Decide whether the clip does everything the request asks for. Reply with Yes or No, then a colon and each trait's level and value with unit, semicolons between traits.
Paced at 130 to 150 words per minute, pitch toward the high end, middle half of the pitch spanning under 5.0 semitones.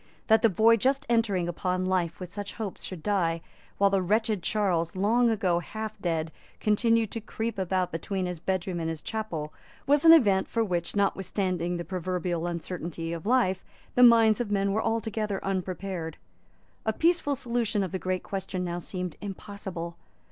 No: average, 170 wpm; high, 195 Hz; average, 3.8 semitones